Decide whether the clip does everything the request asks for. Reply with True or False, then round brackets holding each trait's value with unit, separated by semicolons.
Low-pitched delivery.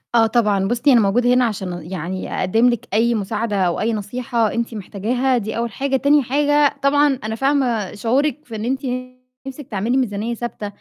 False (235 Hz)